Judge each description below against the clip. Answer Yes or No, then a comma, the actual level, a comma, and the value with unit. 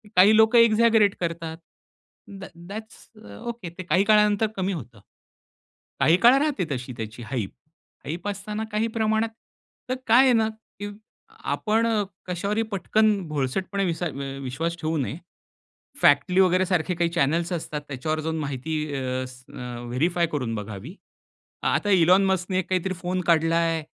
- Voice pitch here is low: No, medium, 175 Hz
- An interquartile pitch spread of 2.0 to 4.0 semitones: No, wide, 5.5 semitones